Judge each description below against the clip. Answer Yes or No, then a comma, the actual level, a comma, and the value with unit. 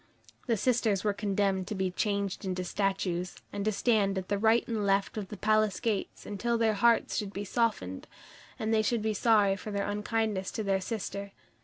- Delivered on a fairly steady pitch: Yes, narrow, 2.0 semitones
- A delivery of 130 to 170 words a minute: No, average, 195 wpm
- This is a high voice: Yes, high, 205 Hz